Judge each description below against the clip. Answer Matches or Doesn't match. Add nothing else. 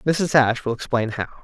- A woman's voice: Doesn't match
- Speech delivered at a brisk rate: Matches